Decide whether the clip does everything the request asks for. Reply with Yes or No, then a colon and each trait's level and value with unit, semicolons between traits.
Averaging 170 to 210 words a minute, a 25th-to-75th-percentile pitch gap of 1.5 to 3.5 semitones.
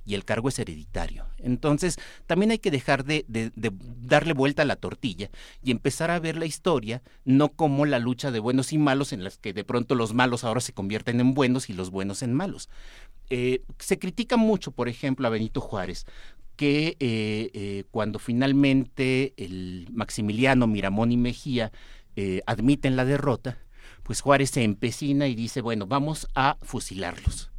No: average, 180 wpm; average, 4.1 semitones